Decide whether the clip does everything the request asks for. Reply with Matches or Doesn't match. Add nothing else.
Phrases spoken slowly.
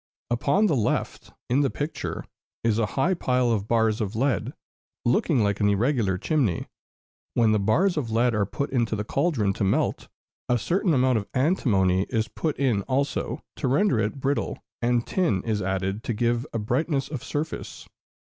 Doesn't match